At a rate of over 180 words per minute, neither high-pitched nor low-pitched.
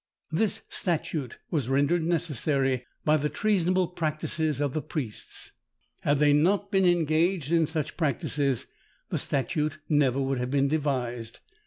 No: average, 140 wpm; medium, 150 Hz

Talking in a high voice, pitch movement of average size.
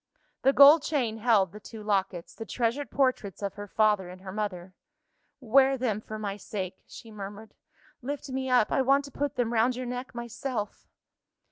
Yes: high, 225 Hz; average, 4.0 semitones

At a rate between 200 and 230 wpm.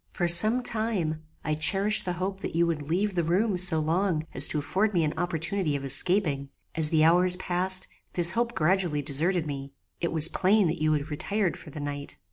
Yes: fast, 205 wpm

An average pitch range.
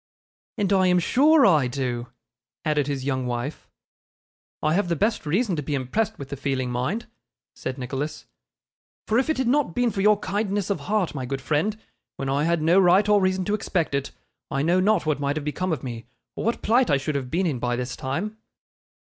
No: wide, 6.9 semitones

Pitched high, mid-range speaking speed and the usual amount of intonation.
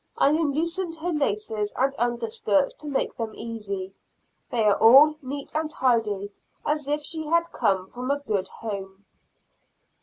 No: very high, 250 Hz; average, 150 wpm; wide, 6.2 semitones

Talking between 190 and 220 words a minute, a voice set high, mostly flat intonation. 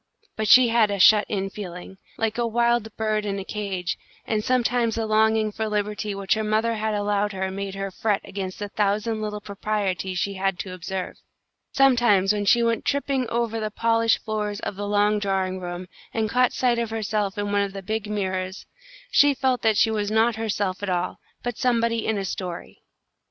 Yes: average, 200 wpm; high, 210 Hz; narrow, 2.3 semitones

